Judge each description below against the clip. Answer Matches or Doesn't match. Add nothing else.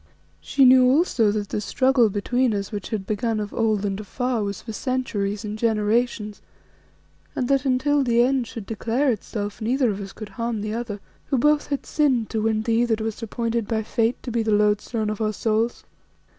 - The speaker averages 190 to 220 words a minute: Matches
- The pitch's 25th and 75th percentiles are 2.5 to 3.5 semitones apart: Matches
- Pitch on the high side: Matches